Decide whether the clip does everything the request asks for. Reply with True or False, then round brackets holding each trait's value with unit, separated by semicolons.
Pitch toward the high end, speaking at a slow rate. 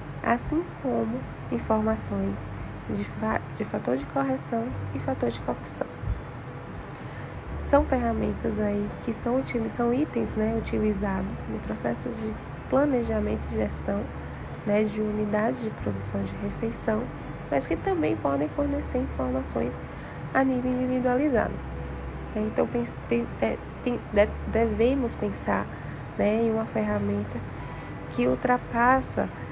True (205 Hz; 105 wpm)